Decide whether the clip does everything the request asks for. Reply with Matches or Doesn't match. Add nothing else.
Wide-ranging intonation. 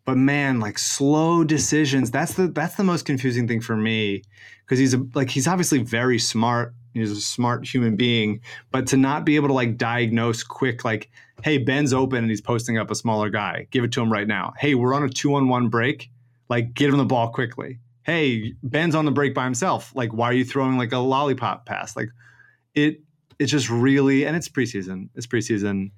Doesn't match